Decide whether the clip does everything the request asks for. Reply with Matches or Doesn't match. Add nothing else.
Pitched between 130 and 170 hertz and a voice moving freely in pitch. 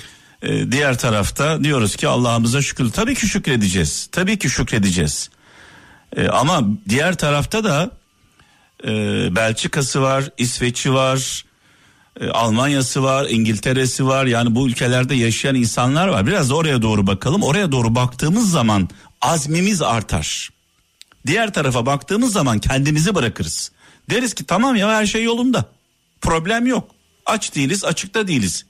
Matches